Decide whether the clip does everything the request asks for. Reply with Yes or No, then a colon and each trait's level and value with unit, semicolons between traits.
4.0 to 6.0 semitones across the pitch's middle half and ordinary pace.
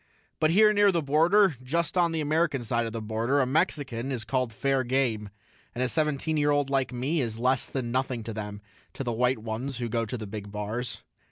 No: average, 4.4 semitones; fast, 225 wpm